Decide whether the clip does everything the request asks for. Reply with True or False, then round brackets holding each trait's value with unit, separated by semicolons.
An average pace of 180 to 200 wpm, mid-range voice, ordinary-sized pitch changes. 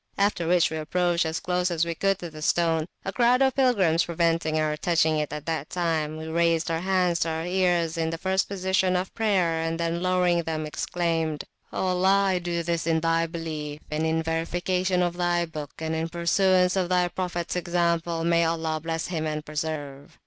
False (195 wpm; 170 Hz; 2.0 semitones)